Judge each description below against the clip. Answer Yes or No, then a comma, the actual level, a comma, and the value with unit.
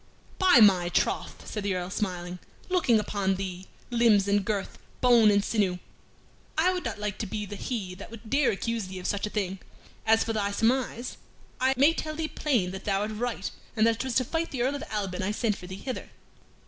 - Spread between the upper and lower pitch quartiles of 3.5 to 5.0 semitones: Yes, average, 4.0 semitones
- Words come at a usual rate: No, fast, 220 wpm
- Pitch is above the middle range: Yes, high, 210 Hz